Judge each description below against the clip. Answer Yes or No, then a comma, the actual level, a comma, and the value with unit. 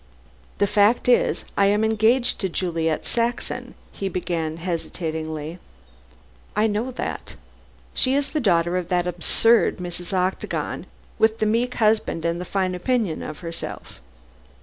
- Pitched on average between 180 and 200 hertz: Yes, high, 190 Hz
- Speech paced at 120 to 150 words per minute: Yes, average, 140 wpm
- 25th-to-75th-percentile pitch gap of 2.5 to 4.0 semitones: No, average, 4.6 semitones